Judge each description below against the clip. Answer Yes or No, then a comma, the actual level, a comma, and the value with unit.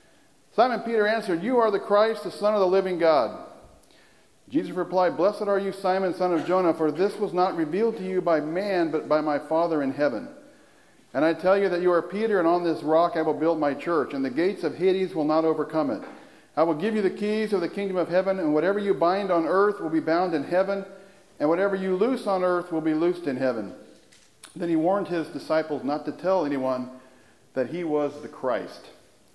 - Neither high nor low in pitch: Yes, medium, 175 Hz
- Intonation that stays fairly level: No, average, 3.9 semitones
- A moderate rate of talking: No, fast, 225 wpm